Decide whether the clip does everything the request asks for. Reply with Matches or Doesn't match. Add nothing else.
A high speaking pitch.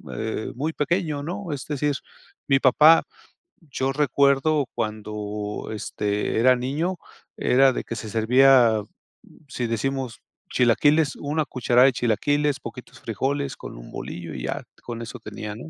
Doesn't match